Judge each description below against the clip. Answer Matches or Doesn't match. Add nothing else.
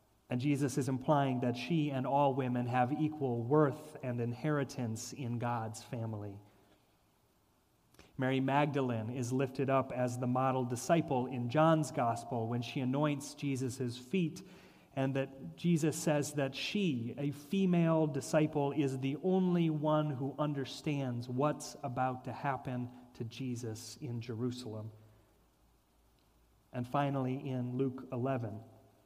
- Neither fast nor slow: Doesn't match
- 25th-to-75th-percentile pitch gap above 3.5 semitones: Doesn't match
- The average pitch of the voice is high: Doesn't match